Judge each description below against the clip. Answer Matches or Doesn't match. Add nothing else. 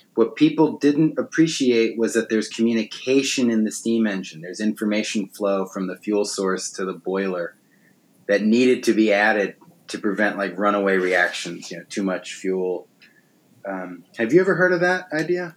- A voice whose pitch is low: Matches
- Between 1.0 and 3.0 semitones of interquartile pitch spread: Doesn't match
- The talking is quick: Doesn't match